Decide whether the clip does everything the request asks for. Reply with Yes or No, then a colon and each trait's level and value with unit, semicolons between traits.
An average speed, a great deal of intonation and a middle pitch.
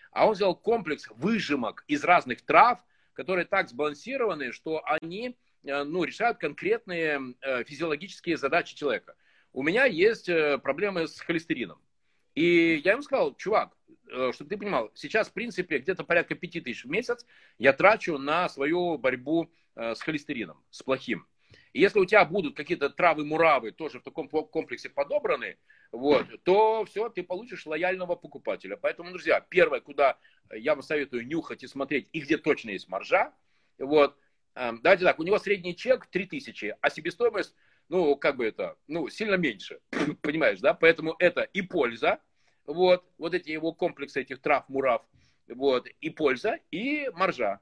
Yes: average, 150 wpm; wide, 6.1 semitones; medium, 175 Hz